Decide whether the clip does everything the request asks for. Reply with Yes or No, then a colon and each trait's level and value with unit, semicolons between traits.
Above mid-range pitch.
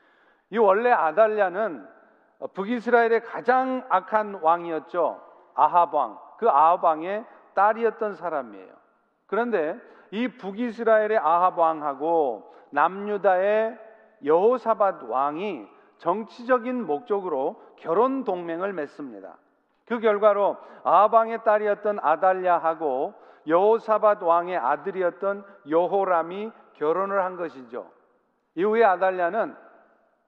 Yes: high, 200 Hz